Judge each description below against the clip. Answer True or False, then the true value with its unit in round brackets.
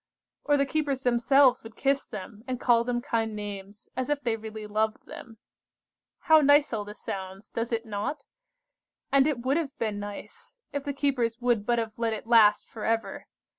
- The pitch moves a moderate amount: True (4.1 semitones)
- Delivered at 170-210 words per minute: True (190 wpm)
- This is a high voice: True (235 Hz)